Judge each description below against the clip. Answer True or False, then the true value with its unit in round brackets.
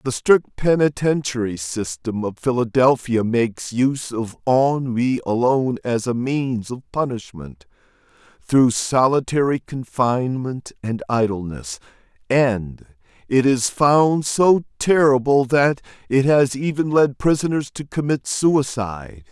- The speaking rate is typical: False (110 wpm)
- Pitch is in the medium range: False (130 Hz)